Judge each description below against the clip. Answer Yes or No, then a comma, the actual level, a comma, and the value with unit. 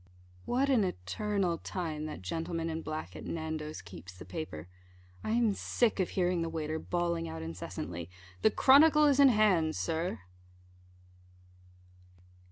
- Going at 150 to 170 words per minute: No, average, 140 wpm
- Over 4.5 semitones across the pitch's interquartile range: Yes, average, 5.3 semitones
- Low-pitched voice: No, medium, 165 Hz